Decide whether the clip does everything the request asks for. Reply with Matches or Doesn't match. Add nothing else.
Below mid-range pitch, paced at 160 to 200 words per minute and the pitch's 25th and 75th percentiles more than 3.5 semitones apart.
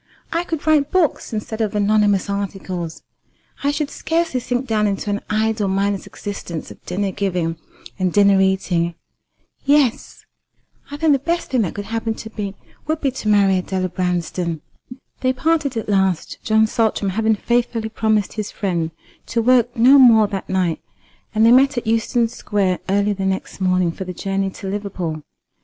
Doesn't match